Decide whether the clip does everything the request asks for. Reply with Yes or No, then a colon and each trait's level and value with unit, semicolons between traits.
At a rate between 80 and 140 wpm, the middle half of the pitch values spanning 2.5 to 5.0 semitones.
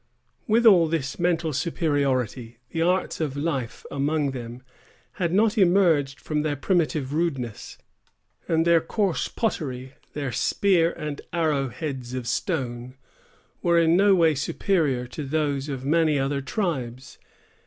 Yes: slow, 135 wpm; average, 4.1 semitones